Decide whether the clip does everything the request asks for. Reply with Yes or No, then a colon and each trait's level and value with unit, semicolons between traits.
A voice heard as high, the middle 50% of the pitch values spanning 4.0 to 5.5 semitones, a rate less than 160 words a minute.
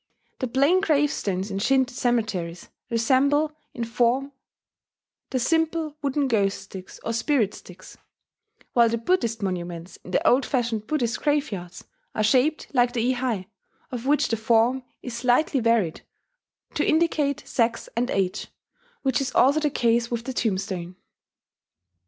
Yes: high, 240 Hz; average, 4.3 semitones; average, 140 wpm